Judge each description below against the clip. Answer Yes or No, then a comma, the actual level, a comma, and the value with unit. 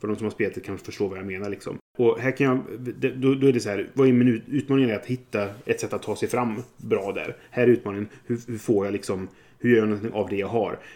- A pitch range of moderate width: Yes, average, 3.8 semitones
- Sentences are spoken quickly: Yes, fast, 285 wpm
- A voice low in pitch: Yes, low, 115 Hz